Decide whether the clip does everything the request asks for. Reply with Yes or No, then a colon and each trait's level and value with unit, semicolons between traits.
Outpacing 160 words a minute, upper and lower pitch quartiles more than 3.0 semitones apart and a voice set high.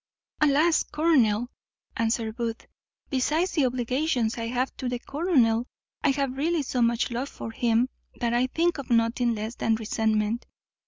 No: average, 155 wpm; average, 3.4 semitones; high, 245 Hz